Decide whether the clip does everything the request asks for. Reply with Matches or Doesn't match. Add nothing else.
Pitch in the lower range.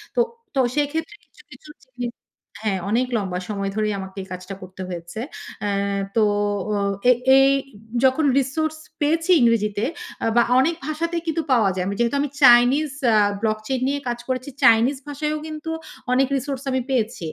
Doesn't match